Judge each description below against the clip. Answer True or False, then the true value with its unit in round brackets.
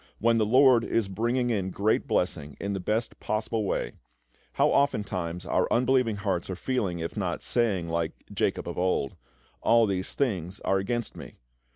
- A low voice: True (105 Hz)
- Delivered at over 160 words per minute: True (170 wpm)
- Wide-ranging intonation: False (4.3 semitones)